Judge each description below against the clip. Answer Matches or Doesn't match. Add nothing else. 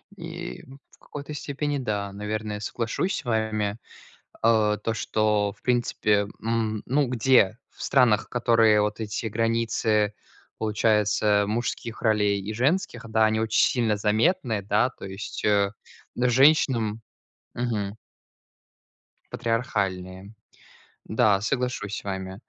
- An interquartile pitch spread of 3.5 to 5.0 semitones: Doesn't match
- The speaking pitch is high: Doesn't match